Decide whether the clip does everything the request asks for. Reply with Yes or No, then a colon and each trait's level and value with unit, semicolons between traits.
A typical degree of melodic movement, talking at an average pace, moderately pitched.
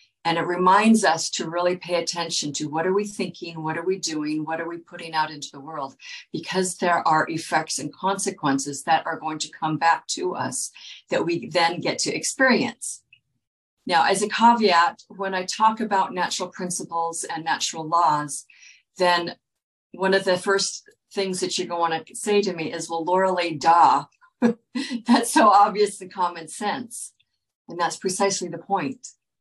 Yes: average, 3.4 semitones; average, 180 wpm; medium, 175 Hz